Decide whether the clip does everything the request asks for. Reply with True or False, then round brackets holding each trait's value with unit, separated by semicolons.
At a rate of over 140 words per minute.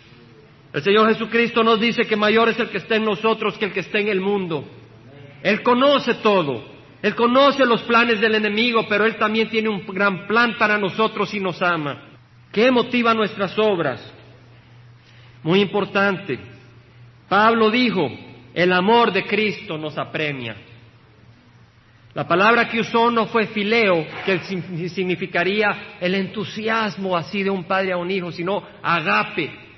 True (150 wpm)